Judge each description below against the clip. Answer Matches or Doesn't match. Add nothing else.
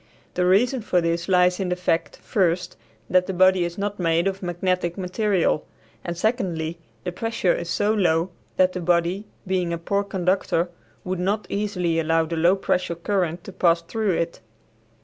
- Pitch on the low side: Doesn't match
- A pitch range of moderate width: Doesn't match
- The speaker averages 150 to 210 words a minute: Matches